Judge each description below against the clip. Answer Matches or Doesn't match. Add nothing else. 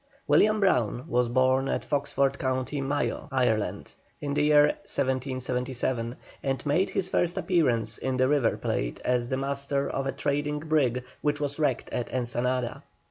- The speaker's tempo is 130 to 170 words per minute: Matches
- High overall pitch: Doesn't match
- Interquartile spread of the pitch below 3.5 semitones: Matches